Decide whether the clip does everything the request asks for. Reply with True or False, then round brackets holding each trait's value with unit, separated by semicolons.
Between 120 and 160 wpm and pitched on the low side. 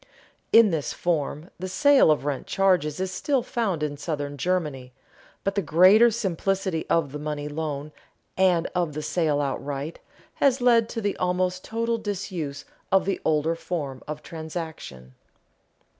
False (150 wpm; 170 Hz)